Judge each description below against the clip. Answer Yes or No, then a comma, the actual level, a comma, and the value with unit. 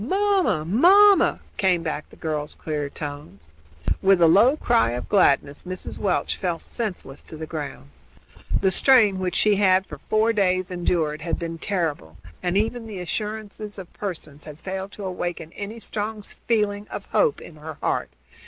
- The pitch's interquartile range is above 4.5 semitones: Yes, average, 5.0 semitones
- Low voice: No, medium, 185 Hz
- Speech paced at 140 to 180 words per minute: Yes, average, 170 wpm